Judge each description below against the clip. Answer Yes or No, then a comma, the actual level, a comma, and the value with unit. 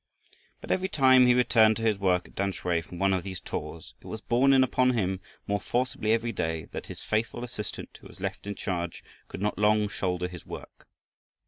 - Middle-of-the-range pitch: No, low, 105 Hz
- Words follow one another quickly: Yes, fast, 210 wpm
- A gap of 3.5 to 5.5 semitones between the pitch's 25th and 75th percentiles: Yes, average, 4.3 semitones